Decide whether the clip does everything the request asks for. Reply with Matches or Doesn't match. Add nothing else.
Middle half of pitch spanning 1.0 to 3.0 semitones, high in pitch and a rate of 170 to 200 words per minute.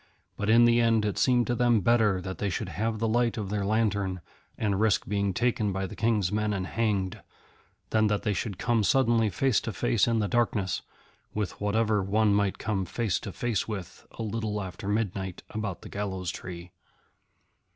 Doesn't match